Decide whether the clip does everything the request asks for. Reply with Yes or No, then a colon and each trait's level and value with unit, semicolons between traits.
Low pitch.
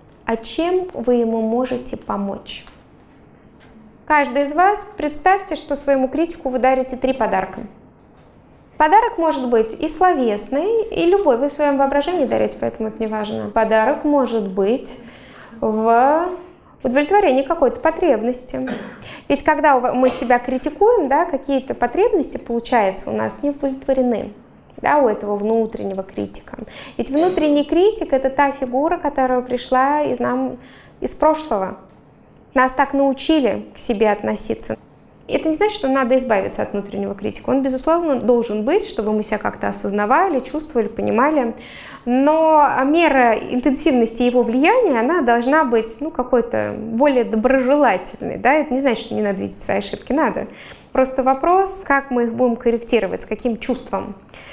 No: very high, 260 Hz